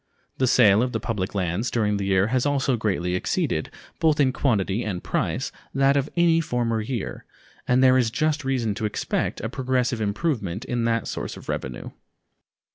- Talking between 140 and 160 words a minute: No, average, 180 wpm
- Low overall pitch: Yes, low, 120 Hz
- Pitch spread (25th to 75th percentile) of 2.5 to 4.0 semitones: No, average, 4.4 semitones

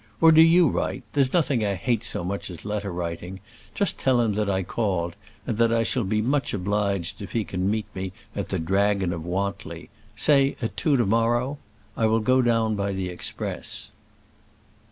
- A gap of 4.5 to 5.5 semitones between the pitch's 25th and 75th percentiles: No, average, 3.9 semitones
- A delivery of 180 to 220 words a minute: Yes, average, 195 wpm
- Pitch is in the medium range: No, low, 105 Hz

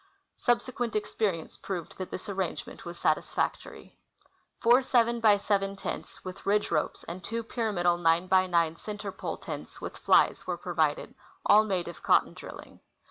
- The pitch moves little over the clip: No, average, 4.2 semitones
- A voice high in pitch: Yes, high, 195 Hz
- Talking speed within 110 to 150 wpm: No, average, 165 wpm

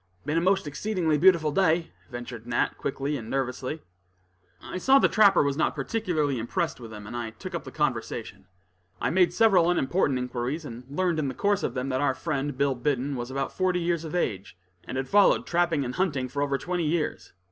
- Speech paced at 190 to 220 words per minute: Yes, fast, 205 wpm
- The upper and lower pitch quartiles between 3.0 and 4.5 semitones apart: No, wide, 5.4 semitones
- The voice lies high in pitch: No, medium, 145 Hz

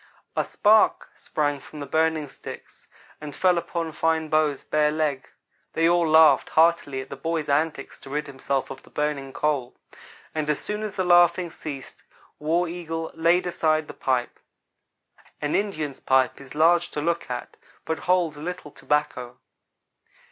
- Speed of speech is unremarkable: Yes, average, 160 wpm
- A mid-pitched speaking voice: Yes, medium, 155 Hz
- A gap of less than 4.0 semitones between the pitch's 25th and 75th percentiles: Yes, average, 2.7 semitones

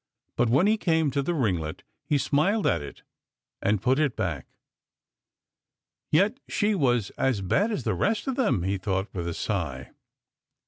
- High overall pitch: No, low, 135 Hz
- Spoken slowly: No, average, 175 wpm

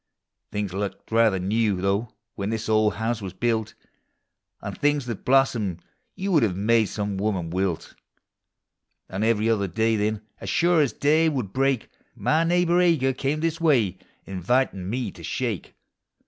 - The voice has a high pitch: No, low, 110 Hz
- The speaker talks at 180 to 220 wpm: No, average, 160 wpm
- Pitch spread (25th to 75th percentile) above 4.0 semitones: Yes, average, 5.2 semitones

